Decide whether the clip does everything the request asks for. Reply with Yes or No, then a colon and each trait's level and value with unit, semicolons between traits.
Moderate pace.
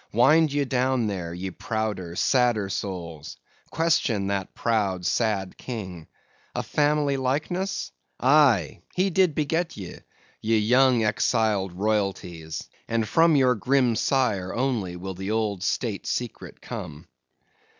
No: slow, 125 wpm